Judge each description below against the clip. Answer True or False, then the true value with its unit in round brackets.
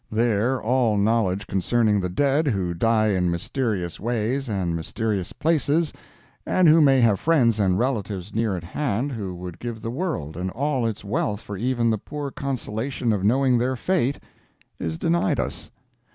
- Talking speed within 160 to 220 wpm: True (165 wpm)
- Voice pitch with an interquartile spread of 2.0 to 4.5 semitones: False (5.2 semitones)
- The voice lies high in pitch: False (115 Hz)